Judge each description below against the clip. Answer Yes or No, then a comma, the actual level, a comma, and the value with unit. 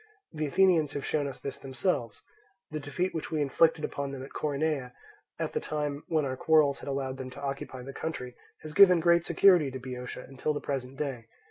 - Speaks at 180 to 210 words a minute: Yes, fast, 205 wpm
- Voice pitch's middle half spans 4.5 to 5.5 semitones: No, average, 2.9 semitones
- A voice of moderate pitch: Yes, medium, 145 Hz